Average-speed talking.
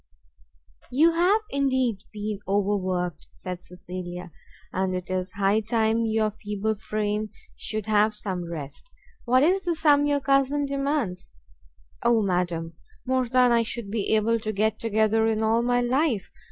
Yes: average, 150 wpm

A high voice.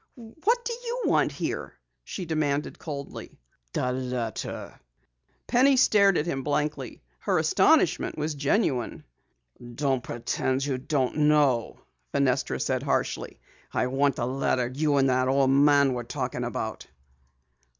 No: medium, 140 Hz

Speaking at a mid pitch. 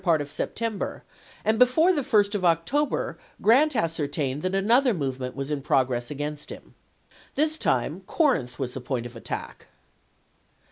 Yes: medium, 165 Hz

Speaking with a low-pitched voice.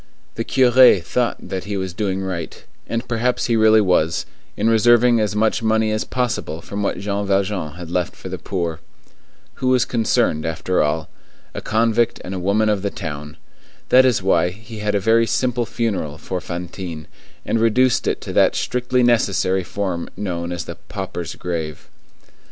Yes: low, 100 Hz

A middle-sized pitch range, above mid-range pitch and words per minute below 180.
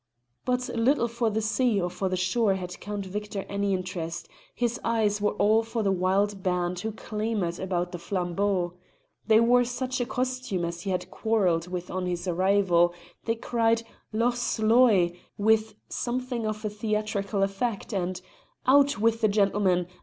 Yes: average, 3.7 semitones; high, 205 Hz; average, 160 wpm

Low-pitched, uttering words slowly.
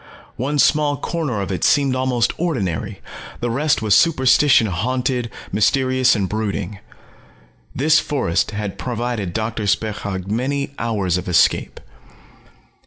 Yes: low, 115 Hz; slow, 120 wpm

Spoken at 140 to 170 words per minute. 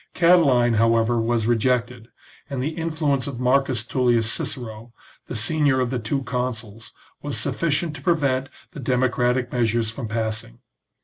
Yes: average, 150 wpm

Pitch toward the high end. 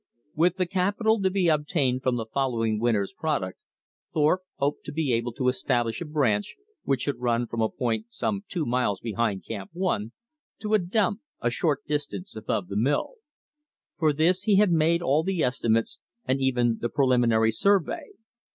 No: low, 135 Hz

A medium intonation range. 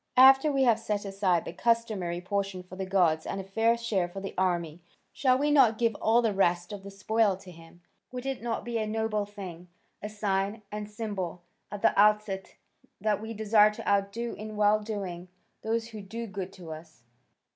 Yes: average, 3.0 semitones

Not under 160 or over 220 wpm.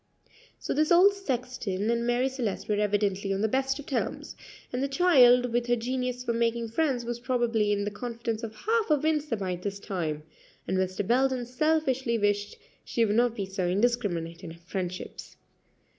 Yes: average, 185 wpm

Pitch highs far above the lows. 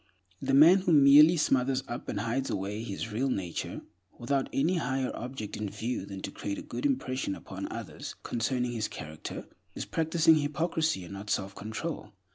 Yes: wide, 6.0 semitones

